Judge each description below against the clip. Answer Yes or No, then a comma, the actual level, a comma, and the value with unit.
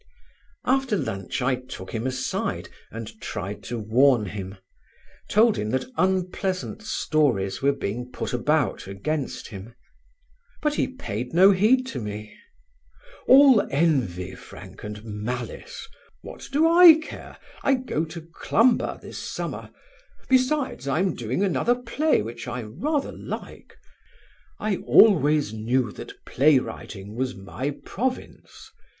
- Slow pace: Yes, slow, 130 wpm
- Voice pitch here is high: No, medium, 140 Hz